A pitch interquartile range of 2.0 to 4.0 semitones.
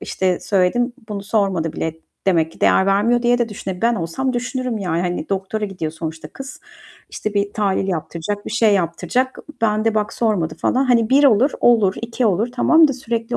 No: average, 4.5 semitones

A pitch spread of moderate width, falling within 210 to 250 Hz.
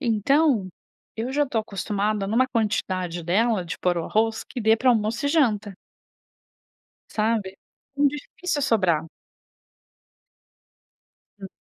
Yes: average, 4.5 semitones; high, 220 Hz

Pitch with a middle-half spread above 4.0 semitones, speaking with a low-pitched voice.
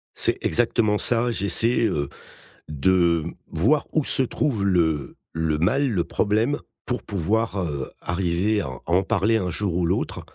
Yes: average, 5.2 semitones; very low, 95 Hz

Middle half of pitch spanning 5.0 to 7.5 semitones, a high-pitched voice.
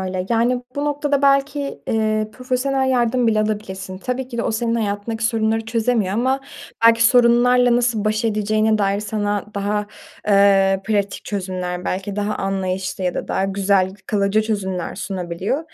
No: average, 3.5 semitones; high, 215 Hz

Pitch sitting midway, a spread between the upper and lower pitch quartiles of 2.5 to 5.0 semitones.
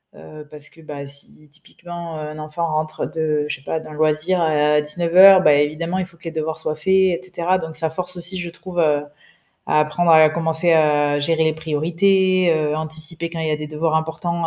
No: medium, 160 Hz; narrow, 2.0 semitones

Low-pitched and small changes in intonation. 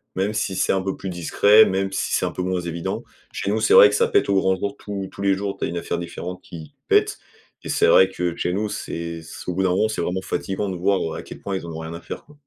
Yes: very low, 95 Hz; narrow, 2.3 semitones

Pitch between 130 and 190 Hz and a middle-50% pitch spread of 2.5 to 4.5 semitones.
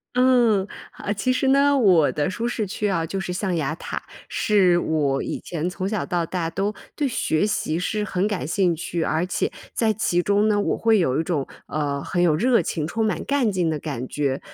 No: medium, 185 Hz; average, 4.9 semitones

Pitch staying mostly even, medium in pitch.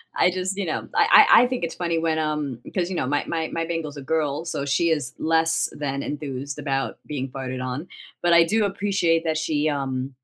No: average, 3.3 semitones; medium, 155 Hz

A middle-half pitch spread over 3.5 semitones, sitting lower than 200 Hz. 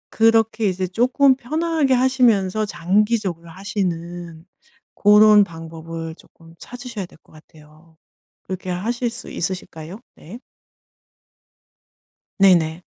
Yes: wide, 5.4 semitones; high, 190 Hz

